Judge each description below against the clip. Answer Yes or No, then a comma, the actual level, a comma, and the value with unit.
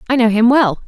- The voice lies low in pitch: No, high, 235 Hz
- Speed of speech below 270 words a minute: No, fast, 275 wpm